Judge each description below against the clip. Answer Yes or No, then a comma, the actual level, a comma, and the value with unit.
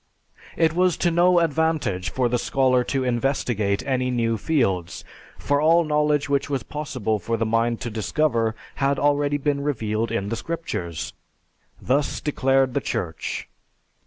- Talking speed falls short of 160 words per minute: Yes, average, 150 wpm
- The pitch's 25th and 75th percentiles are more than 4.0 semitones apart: Yes, average, 4.4 semitones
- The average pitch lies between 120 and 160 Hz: Yes, low, 135 Hz